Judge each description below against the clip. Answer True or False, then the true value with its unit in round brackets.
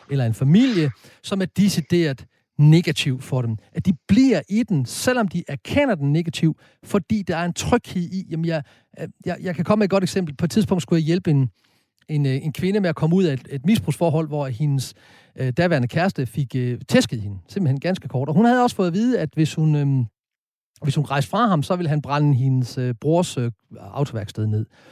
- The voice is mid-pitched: True (155 Hz)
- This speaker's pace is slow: False (220 wpm)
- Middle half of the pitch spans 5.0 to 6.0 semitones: True (5.4 semitones)